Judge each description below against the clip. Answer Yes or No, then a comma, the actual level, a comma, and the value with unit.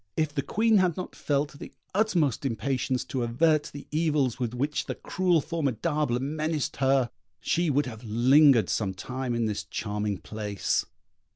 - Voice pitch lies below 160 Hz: Yes, low, 135 Hz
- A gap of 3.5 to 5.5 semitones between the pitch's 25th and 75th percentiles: Yes, average, 4.6 semitones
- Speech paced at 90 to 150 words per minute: No, average, 160 wpm